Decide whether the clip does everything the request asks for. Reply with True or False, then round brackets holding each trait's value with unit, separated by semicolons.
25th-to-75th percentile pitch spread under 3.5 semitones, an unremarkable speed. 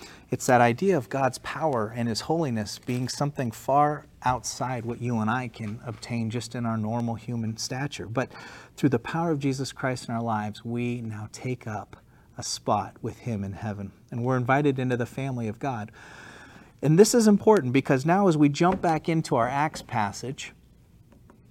False (3.9 semitones; 185 wpm)